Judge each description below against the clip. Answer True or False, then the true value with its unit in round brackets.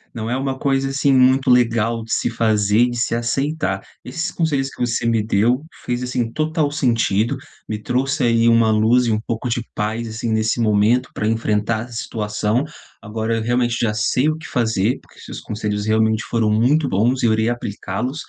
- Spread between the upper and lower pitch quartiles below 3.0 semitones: True (2.6 semitones)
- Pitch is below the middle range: True (115 Hz)